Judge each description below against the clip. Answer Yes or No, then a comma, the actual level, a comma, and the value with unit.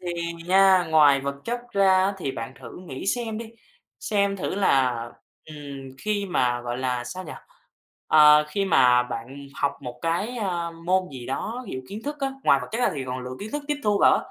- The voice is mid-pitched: Yes, medium, 165 Hz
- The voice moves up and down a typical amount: No, wide, 7.1 semitones